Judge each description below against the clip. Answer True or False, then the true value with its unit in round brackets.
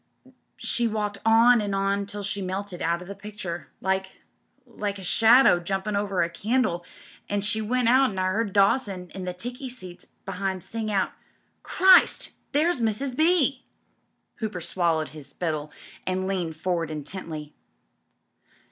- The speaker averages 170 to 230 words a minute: False (160 wpm)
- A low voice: False (200 Hz)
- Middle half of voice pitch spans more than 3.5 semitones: True (3.9 semitones)